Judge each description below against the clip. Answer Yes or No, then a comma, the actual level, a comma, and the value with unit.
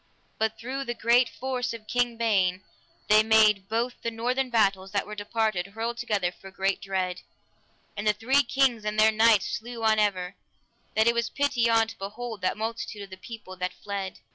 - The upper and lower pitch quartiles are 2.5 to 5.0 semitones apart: Yes, average, 2.9 semitones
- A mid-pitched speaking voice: No, high, 220 Hz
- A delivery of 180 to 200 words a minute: Yes, average, 190 wpm